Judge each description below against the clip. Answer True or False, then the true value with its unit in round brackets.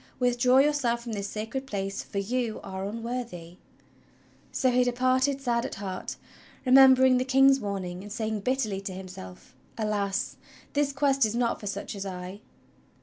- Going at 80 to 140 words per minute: False (160 wpm)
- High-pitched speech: True (230 Hz)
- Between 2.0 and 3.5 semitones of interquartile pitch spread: False (4.5 semitones)